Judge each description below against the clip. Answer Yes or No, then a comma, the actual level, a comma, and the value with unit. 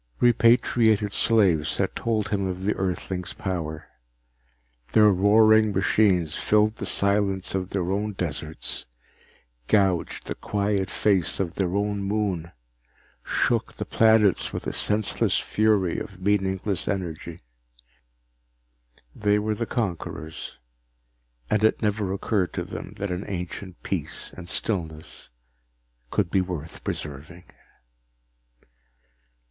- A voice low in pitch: Yes, low, 100 Hz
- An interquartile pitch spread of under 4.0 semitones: Yes, average, 2.9 semitones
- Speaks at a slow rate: Yes, slow, 115 wpm